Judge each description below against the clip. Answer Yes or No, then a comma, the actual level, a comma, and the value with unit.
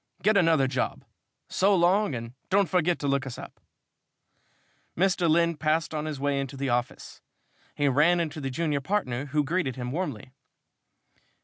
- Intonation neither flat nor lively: Yes, average, 4.4 semitones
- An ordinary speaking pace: Yes, average, 165 wpm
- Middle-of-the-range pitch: Yes, medium, 150 Hz